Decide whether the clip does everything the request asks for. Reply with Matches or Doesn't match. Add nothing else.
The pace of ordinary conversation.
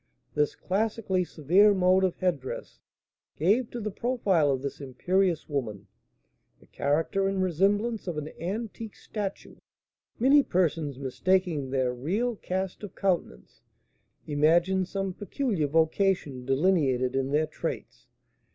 Doesn't match